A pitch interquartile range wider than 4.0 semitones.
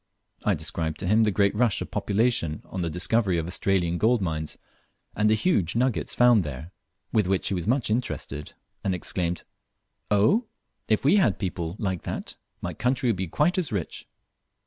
Yes: average, 5.1 semitones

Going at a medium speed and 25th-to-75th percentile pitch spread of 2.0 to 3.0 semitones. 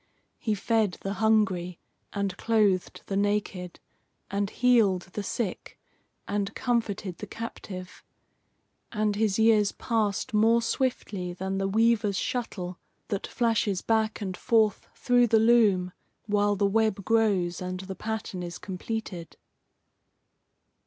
No: slow, 125 wpm; average, 2.7 semitones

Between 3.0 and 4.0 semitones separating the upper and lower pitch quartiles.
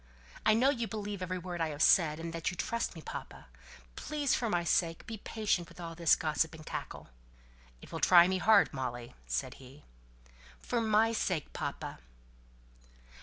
No: average, 5.1 semitones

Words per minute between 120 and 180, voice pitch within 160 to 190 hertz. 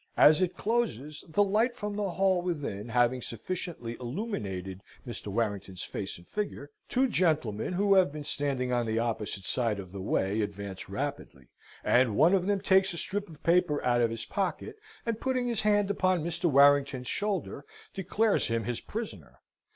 No: average, 175 wpm; medium, 145 Hz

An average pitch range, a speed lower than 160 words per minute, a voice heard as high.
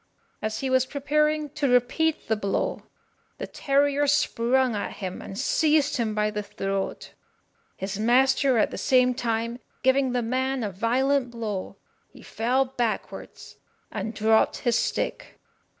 Yes: average, 3.8 semitones; average, 145 wpm; very high, 250 Hz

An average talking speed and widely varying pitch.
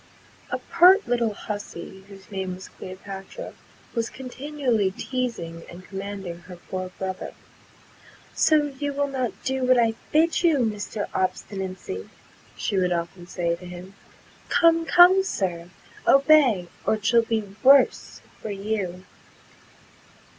No: slow, 130 wpm; wide, 6.1 semitones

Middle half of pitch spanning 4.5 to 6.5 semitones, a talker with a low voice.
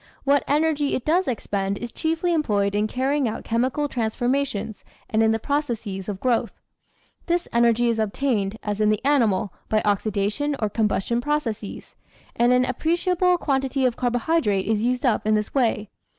No: average, 5.0 semitones; high, 240 Hz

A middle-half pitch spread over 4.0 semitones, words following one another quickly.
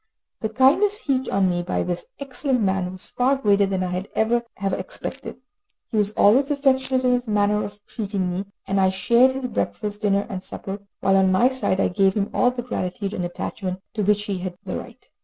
Yes: average, 4.7 semitones; fast, 215 wpm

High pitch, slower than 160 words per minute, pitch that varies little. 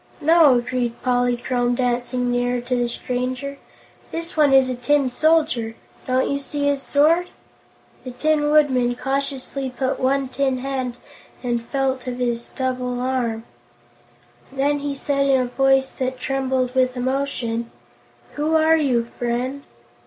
Yes: very high, 260 Hz; average, 145 wpm; narrow, 2.1 semitones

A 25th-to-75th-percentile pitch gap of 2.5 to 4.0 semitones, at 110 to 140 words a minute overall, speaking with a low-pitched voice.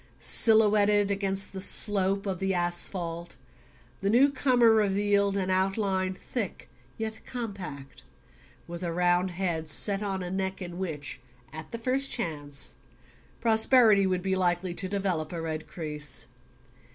No: average, 2.9 semitones; slow, 135 wpm; high, 190 Hz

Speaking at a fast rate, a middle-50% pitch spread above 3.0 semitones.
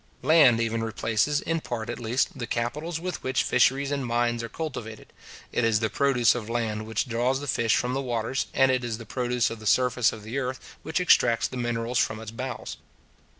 No: fast, 210 wpm; narrow, 2.6 semitones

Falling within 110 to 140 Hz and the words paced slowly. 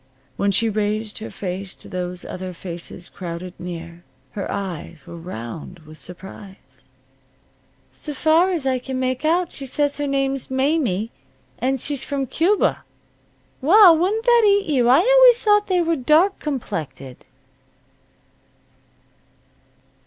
No: very high, 255 Hz; slow, 130 wpm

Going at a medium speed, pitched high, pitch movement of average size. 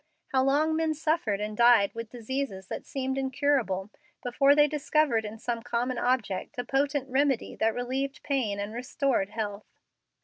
Yes: average, 160 wpm; very high, 250 Hz; average, 3.9 semitones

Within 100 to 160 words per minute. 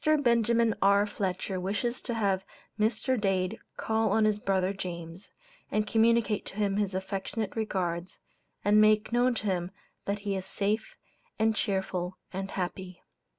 Yes: average, 150 wpm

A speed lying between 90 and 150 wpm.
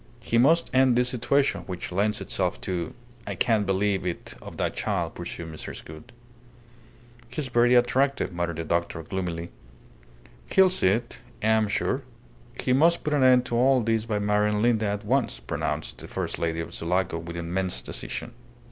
No: average, 175 wpm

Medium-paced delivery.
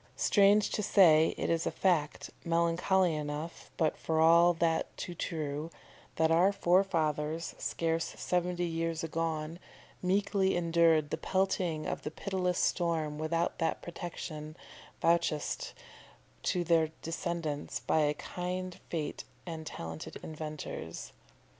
No: slow, 120 wpm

